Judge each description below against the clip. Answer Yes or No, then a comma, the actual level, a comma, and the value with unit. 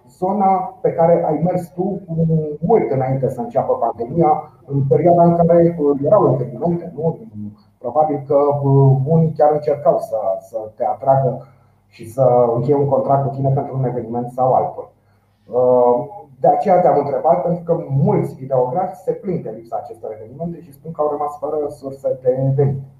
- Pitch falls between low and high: Yes, medium, 145 Hz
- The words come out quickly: No, average, 160 wpm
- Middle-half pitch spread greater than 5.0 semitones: No, average, 4.7 semitones